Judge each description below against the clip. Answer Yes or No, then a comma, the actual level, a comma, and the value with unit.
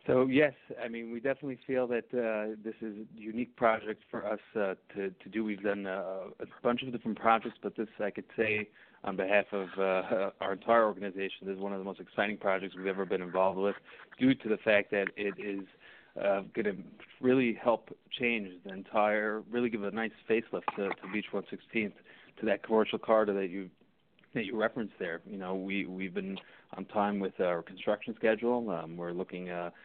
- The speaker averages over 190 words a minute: Yes, fast, 205 wpm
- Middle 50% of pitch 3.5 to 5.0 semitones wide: No, average, 2.9 semitones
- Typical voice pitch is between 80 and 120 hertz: Yes, low, 105 Hz